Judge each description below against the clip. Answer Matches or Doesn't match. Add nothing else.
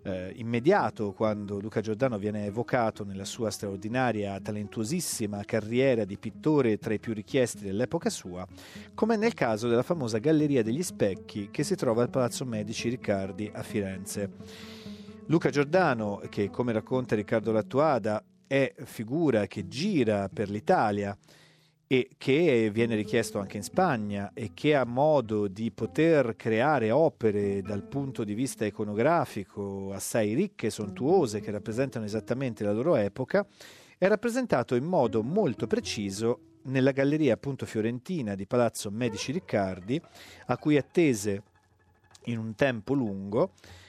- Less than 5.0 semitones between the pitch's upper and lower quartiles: Matches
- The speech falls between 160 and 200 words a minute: Doesn't match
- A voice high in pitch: Doesn't match